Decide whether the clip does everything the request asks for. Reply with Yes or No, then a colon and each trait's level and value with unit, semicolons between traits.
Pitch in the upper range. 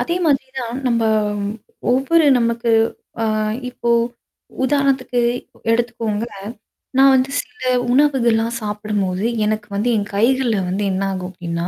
Yes: high, 235 Hz